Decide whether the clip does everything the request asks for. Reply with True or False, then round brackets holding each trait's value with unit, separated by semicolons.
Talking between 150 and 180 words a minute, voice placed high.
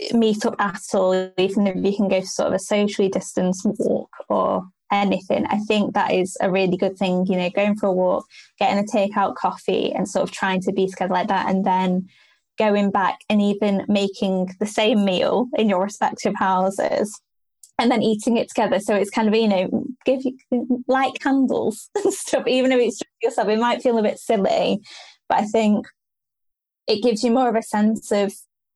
False (205 wpm; 210 Hz)